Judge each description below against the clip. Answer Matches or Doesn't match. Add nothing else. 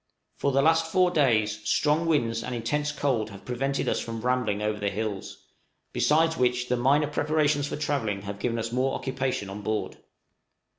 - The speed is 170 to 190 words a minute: Matches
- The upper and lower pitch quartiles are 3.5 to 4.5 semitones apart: Doesn't match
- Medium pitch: Doesn't match